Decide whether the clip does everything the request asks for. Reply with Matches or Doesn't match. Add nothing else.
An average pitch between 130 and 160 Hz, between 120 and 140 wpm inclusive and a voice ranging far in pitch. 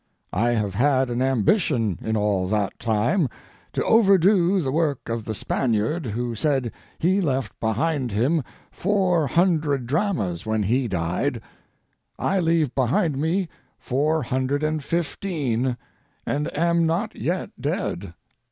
Matches